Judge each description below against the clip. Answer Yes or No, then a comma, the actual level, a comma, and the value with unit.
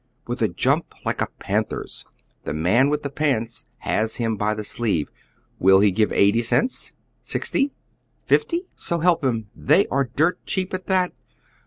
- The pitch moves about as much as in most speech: No, wide, 8.0 semitones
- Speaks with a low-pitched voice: Yes, low, 120 Hz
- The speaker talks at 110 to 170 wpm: Yes, average, 165 wpm